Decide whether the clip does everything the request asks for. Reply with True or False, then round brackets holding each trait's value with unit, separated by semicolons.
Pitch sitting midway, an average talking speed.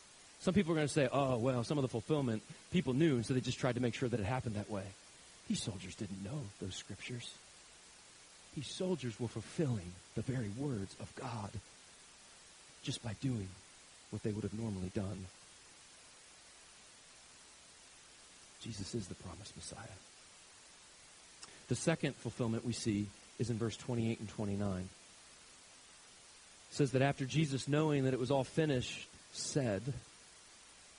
False (120 Hz; 155 wpm)